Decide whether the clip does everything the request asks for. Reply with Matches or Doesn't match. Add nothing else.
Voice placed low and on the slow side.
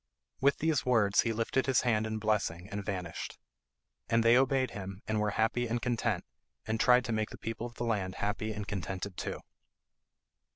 Doesn't match